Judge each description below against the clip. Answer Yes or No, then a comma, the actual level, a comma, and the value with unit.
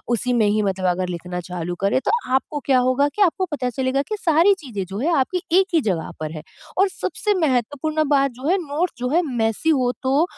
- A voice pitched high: Yes, very high, 260 Hz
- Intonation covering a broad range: Yes, wide, 7.3 semitones